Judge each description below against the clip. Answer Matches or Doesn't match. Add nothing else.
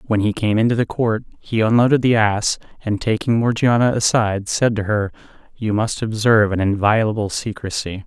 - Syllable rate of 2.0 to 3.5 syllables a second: Doesn't match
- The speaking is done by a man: Matches